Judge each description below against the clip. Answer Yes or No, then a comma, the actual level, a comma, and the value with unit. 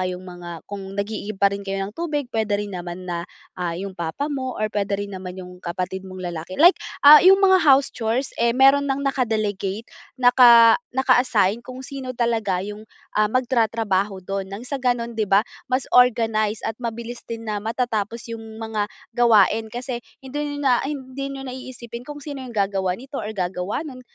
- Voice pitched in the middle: No, high, 225 Hz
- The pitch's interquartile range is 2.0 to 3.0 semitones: No, average, 4.5 semitones